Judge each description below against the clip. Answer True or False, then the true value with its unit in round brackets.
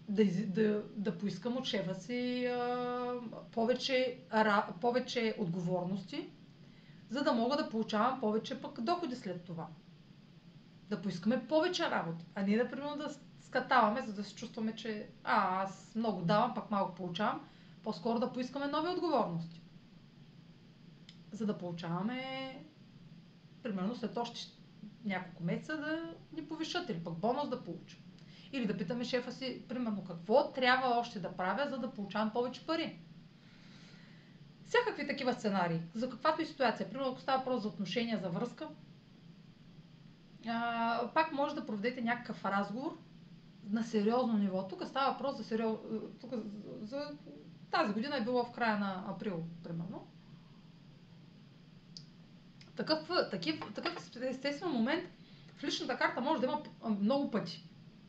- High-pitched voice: True (215 Hz)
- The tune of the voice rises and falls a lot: True (6.0 semitones)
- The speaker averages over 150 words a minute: False (135 wpm)